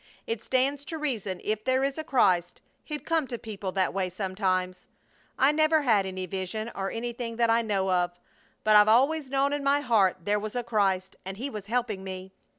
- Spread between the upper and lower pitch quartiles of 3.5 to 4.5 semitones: No, wide, 5.6 semitones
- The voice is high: Yes, high, 215 Hz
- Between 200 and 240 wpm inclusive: Yes, fast, 205 wpm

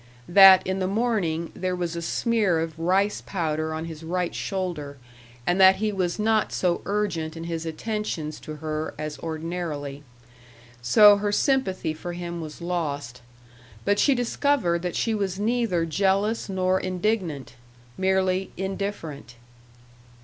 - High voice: No, medium, 180 Hz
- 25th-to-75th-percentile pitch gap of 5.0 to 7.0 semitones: No, average, 3.8 semitones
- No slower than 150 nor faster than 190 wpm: No, average, 140 wpm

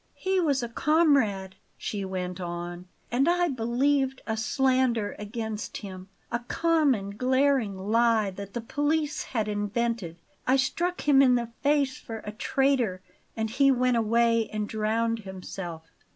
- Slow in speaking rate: No, average, 145 wpm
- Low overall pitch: No, high, 230 Hz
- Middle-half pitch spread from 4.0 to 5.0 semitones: Yes, average, 4.7 semitones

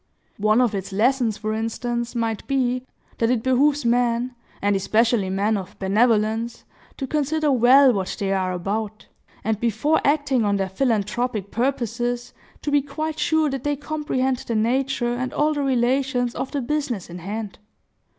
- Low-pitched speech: No, high, 240 Hz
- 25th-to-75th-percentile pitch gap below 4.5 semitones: Yes, average, 3.9 semitones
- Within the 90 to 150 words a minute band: No, average, 160 wpm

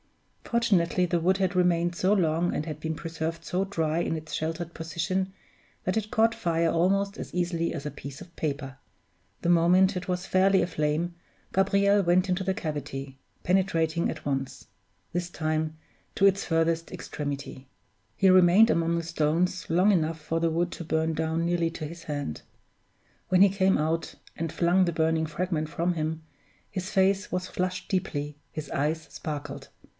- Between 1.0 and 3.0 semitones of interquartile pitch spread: Yes, narrow, 2.6 semitones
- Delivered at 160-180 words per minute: Yes, average, 170 wpm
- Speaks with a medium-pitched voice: Yes, medium, 170 Hz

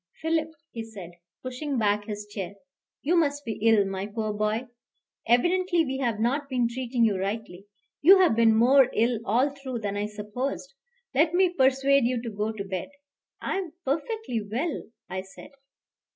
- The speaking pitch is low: No, high, 235 Hz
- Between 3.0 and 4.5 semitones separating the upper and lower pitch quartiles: No, average, 5.0 semitones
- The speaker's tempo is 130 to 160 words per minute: No, average, 170 wpm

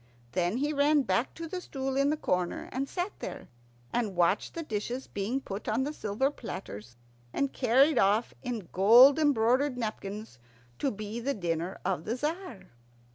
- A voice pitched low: No, high, 240 Hz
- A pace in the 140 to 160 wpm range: No, average, 170 wpm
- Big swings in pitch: Yes, wide, 5.8 semitones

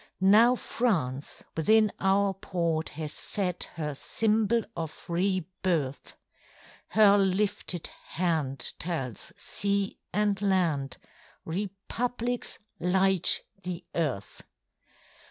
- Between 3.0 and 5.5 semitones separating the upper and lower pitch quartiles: Yes, average, 4.0 semitones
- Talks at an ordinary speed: No, slow, 90 wpm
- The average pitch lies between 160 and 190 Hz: Yes, medium, 185 Hz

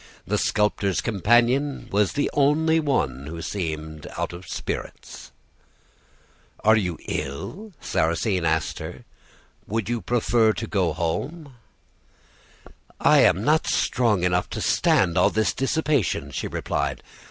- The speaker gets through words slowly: Yes, slow, 125 wpm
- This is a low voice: Yes, low, 105 Hz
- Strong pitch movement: Yes, wide, 7.1 semitones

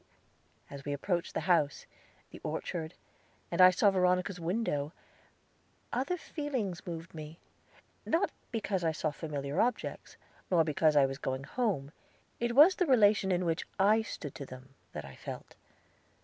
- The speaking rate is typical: Yes, average, 150 wpm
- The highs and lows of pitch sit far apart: Yes, wide, 6.0 semitones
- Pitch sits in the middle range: Yes, medium, 175 Hz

